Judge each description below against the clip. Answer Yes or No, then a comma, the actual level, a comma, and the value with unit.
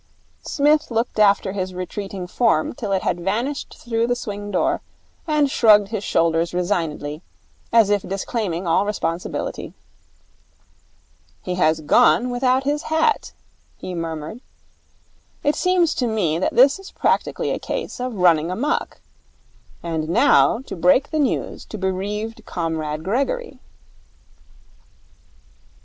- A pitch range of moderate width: No, wide, 6.1 semitones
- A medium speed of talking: No, slow, 130 wpm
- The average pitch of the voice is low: No, high, 205 Hz